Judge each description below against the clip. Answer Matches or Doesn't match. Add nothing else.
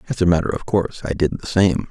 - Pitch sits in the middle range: Doesn't match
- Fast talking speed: Matches